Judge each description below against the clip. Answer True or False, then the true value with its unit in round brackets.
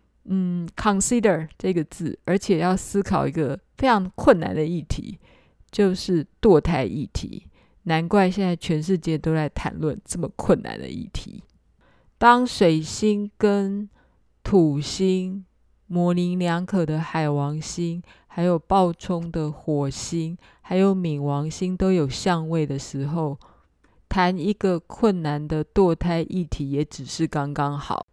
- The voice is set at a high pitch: False (175 Hz)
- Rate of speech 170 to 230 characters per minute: True (210 characters per minute)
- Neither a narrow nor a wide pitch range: True (3.5 semitones)